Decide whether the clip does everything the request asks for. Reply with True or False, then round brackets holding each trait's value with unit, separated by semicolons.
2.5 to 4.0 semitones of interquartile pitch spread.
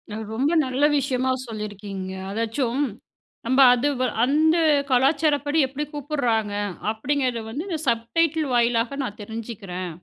False (4.5 semitones)